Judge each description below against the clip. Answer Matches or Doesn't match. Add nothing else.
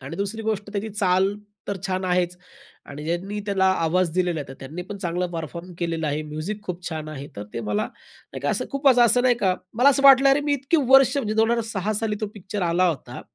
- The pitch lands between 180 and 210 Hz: Matches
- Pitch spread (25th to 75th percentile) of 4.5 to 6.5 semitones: Matches